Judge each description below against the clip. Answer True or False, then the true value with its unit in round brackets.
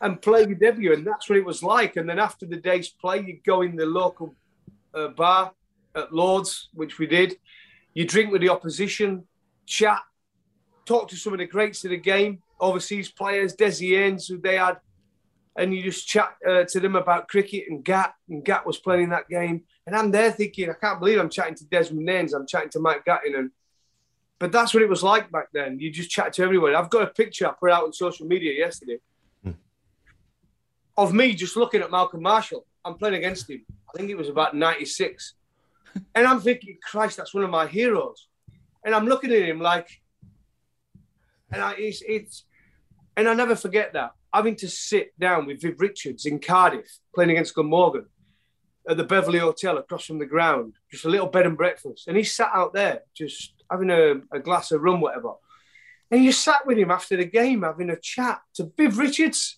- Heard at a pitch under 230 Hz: True (185 Hz)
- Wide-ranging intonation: False (4.1 semitones)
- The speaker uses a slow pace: False (205 wpm)